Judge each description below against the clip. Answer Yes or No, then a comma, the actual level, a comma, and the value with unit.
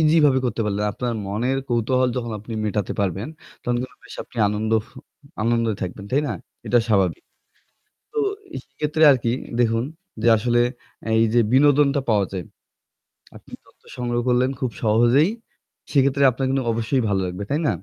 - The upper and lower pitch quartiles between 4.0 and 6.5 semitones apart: No, average, 3.6 semitones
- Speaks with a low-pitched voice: Yes, low, 120 Hz